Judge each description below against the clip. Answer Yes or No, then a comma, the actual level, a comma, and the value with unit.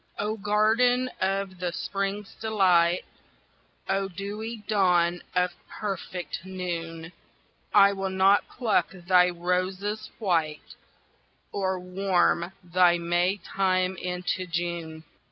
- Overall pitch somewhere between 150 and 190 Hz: Yes, medium, 185 Hz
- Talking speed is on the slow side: Yes, slow, 100 wpm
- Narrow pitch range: Yes, narrow, 2.2 semitones